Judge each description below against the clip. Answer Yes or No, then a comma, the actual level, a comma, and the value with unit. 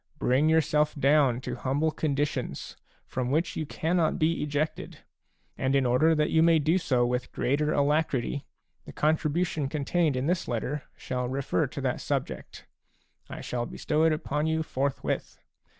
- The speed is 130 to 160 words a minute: Yes, average, 155 wpm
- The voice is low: No, medium, 150 Hz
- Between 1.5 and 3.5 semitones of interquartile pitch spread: Yes, average, 3.2 semitones